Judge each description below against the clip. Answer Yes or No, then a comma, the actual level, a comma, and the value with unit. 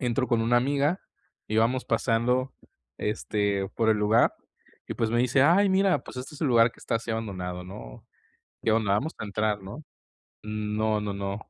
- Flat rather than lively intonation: No, average, 3.4 semitones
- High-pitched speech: No, low, 115 Hz